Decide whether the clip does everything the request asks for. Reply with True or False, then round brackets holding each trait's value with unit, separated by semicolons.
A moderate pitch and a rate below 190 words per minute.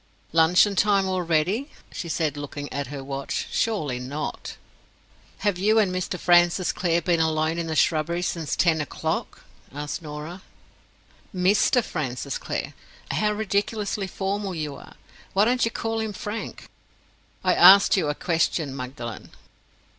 True (175 Hz; 140 wpm)